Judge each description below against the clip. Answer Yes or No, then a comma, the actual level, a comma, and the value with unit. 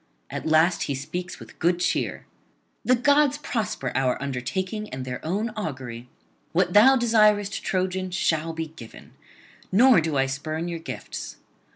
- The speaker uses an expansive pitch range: Yes, wide, 7.0 semitones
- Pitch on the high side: No, medium, 175 Hz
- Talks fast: No, average, 150 wpm